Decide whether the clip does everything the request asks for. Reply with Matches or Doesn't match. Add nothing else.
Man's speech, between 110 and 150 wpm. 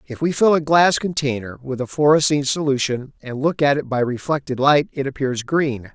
Doesn't match